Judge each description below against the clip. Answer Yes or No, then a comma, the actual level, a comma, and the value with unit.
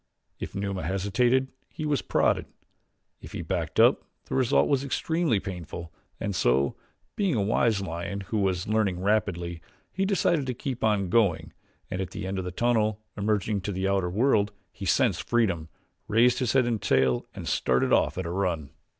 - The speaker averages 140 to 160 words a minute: No, average, 180 wpm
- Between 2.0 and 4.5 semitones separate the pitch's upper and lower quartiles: No, average, 4.9 semitones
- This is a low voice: Yes, low, 100 Hz